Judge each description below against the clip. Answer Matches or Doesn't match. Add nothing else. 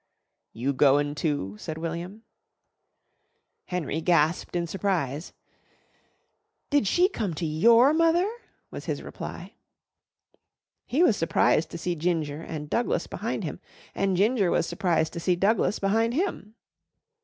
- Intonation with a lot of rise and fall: Matches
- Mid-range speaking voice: Matches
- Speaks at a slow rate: Matches